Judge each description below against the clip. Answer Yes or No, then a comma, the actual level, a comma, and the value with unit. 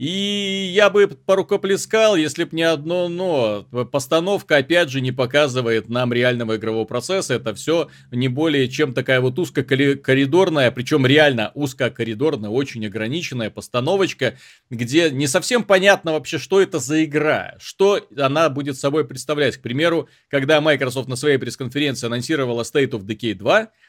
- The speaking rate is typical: Yes, average, 145 wpm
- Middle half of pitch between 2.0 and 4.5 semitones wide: No, average, 4.9 semitones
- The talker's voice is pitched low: No, medium, 145 Hz